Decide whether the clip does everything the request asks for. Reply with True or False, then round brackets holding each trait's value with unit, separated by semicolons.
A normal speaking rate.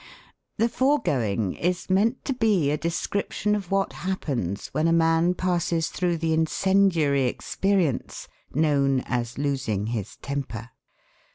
False (125 wpm)